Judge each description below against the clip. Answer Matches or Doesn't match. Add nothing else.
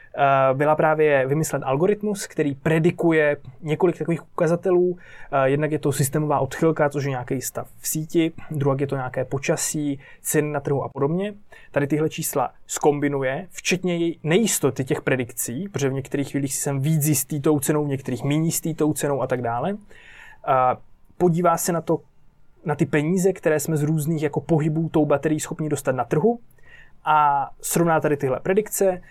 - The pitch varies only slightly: Doesn't match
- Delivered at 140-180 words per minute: Matches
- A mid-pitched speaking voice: Matches